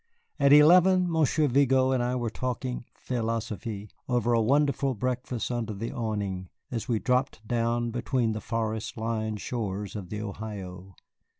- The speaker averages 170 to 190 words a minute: No, average, 145 wpm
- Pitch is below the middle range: Yes, low, 115 Hz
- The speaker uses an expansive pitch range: No, average, 2.9 semitones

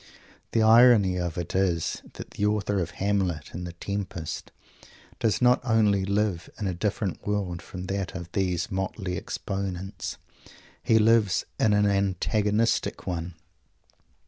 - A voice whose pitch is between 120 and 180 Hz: No, very low, 95 Hz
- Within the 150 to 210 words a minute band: No, average, 140 wpm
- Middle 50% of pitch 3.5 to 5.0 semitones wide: No, average, 2.7 semitones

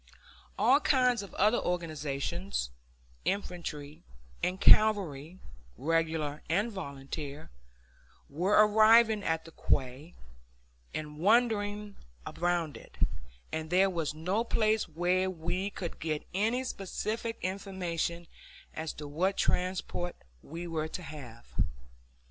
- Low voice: No, medium, 175 Hz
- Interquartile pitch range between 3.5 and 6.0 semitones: Yes, average, 4.6 semitones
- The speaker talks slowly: Yes, slow, 110 wpm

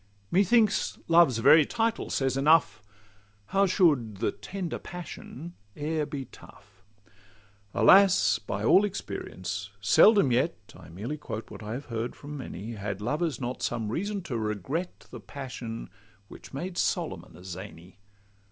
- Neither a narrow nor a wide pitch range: No, wide, 8.3 semitones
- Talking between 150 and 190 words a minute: No, average, 140 wpm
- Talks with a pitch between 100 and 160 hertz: Yes, low, 135 Hz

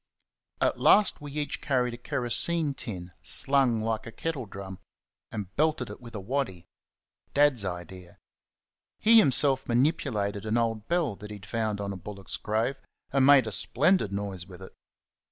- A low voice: Yes, low, 115 Hz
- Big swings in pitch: Yes, wide, 5.7 semitones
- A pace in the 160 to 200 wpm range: Yes, average, 165 wpm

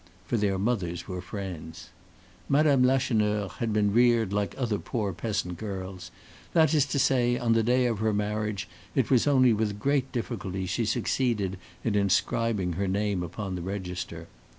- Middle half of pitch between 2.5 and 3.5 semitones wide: No, average, 4.1 semitones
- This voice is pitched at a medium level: No, low, 105 Hz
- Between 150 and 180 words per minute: Yes, average, 165 wpm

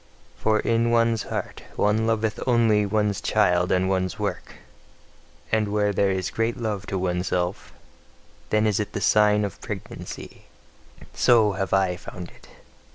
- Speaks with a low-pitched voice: Yes, low, 105 Hz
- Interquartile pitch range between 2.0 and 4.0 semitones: Yes, narrow, 2.6 semitones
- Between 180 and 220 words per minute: No, average, 150 wpm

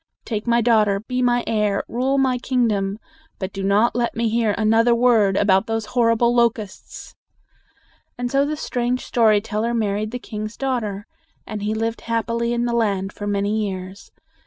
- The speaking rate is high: No, average, 170 wpm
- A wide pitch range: No, narrow, 2.5 semitones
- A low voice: No, high, 225 Hz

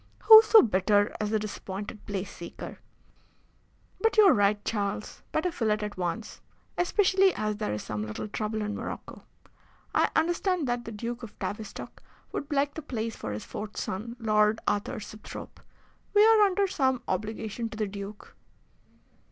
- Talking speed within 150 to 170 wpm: Yes, average, 165 wpm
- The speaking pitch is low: No, high, 215 Hz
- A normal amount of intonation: No, wide, 5.7 semitones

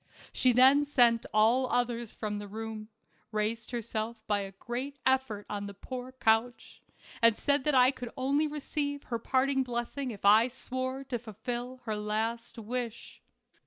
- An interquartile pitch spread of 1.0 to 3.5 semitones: Yes, average, 2.9 semitones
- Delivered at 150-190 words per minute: Yes, average, 160 wpm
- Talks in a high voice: Yes, high, 240 Hz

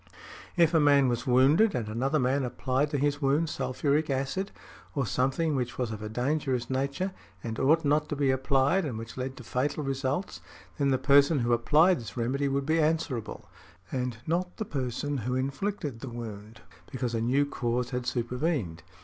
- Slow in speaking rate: No, average, 185 wpm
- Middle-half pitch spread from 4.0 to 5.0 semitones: No, average, 3.1 semitones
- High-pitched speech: No, low, 135 Hz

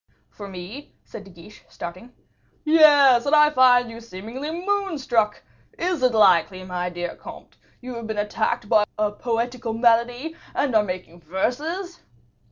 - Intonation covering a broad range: Yes, wide, 5.7 semitones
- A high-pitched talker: Yes, high, 230 Hz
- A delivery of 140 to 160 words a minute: Yes, average, 155 wpm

